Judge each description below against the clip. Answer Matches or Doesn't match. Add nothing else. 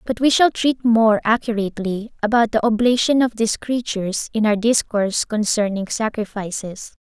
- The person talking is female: Matches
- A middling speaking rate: Matches